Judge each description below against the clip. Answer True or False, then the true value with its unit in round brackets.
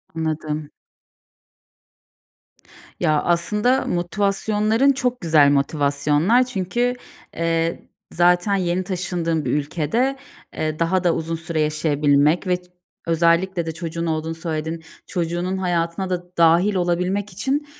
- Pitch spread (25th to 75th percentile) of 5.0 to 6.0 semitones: False (2.9 semitones)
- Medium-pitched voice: True (170 Hz)